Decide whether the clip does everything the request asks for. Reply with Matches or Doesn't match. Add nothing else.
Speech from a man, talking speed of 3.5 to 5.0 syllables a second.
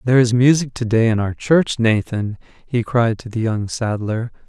Matches